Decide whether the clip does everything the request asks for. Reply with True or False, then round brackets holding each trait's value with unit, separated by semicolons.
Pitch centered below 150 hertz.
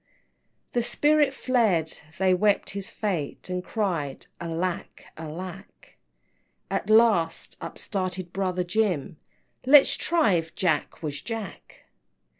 False (185 Hz)